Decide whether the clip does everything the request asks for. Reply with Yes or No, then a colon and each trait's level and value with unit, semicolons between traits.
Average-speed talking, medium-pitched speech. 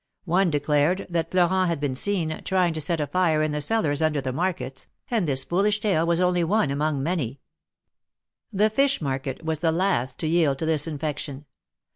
Yes: average, 190 wpm; medium, 160 Hz